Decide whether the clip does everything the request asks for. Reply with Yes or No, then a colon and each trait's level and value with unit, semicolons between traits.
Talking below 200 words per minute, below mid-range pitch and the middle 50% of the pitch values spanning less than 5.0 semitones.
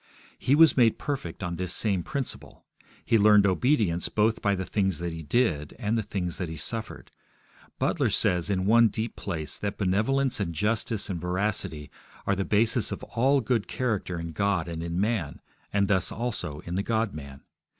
Yes: average, 185 wpm; low, 100 Hz; average, 4.5 semitones